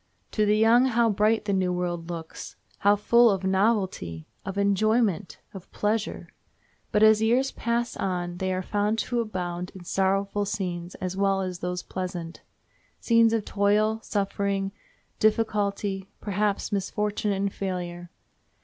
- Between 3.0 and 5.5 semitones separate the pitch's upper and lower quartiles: No, narrow, 2.6 semitones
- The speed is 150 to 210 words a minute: No, average, 140 wpm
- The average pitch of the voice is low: No, high, 200 Hz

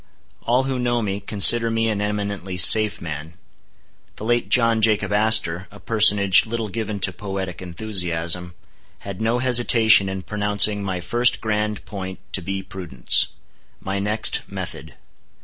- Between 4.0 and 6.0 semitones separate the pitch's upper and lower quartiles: No, average, 2.8 semitones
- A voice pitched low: Yes, low, 105 Hz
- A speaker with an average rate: Yes, average, 145 wpm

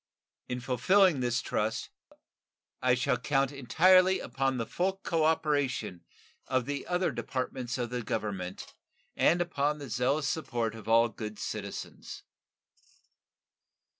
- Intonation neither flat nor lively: Yes, average, 4.4 semitones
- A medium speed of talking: No, slow, 120 wpm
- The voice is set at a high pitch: No, low, 130 Hz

